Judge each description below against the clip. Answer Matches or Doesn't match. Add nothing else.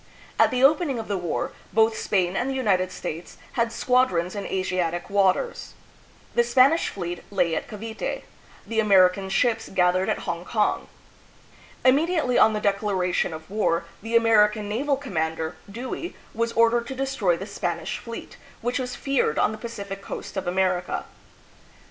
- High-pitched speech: Matches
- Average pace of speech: Matches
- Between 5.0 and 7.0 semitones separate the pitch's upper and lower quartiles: Doesn't match